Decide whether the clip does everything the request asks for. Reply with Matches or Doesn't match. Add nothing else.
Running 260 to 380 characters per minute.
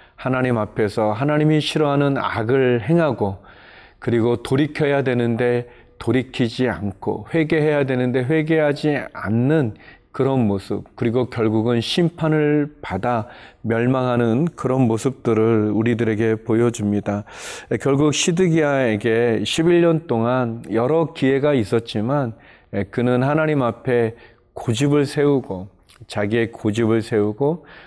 Matches